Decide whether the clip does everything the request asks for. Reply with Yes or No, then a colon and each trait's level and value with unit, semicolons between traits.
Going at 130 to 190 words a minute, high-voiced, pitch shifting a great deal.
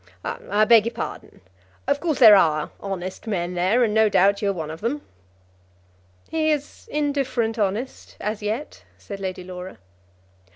No: average, 160 wpm; high, 210 Hz; average, 4.7 semitones